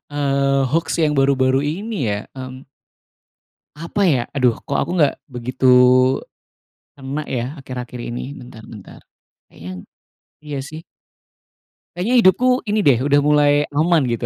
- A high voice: No, medium, 140 Hz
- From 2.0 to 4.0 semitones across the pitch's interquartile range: Yes, average, 3.6 semitones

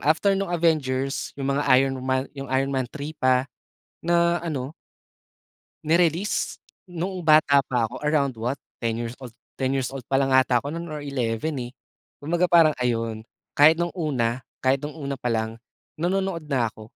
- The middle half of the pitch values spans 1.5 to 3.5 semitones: No, average, 4.0 semitones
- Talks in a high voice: No, medium, 140 Hz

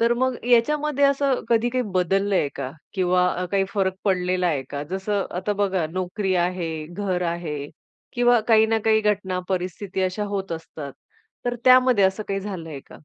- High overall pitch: Yes, high, 195 Hz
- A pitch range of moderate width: Yes, average, 3.7 semitones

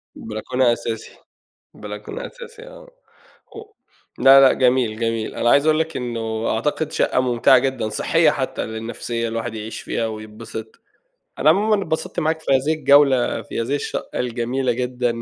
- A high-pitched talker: No, low, 125 Hz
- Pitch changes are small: No, average, 4.4 semitones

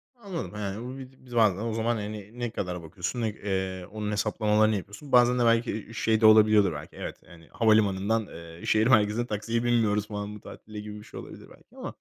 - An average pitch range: No, narrow, 2.1 semitones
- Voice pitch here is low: Yes, low, 110 Hz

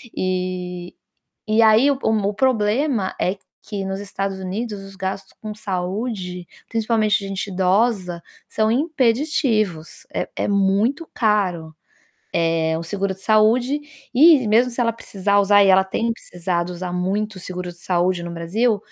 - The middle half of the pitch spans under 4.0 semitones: Yes, average, 3.5 semitones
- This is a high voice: Yes, high, 200 Hz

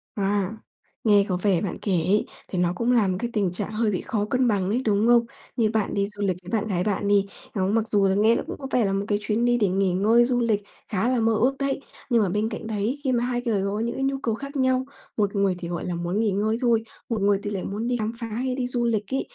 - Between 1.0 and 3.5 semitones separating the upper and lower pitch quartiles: Yes, average, 3.1 semitones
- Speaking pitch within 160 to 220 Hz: Yes, high, 215 Hz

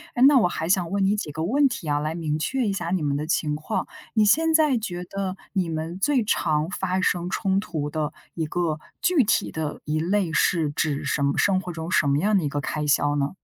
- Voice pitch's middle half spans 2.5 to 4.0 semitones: No, average, 4.5 semitones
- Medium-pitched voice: Yes, medium, 175 Hz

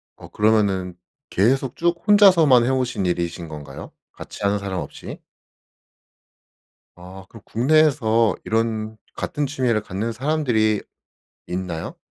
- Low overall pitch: Yes, low, 110 Hz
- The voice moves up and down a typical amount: No, wide, 5.7 semitones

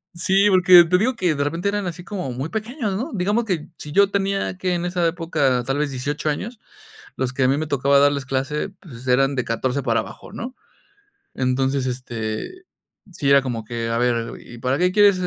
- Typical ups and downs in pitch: No, wide, 6.3 semitones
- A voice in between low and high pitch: Yes, medium, 150 Hz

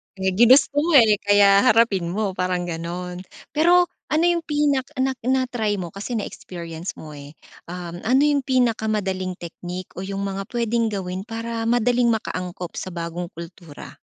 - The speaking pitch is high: Yes, high, 205 Hz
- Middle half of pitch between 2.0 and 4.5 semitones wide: No, wide, 5.4 semitones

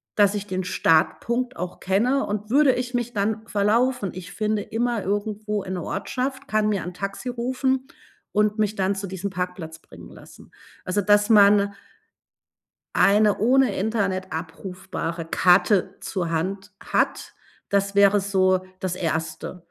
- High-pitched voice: Yes, high, 200 Hz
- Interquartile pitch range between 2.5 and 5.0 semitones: Yes, average, 2.8 semitones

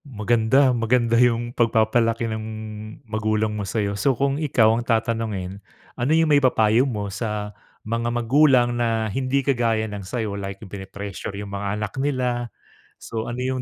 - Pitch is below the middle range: Yes, low, 115 Hz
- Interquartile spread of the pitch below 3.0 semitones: Yes, narrow, 2.5 semitones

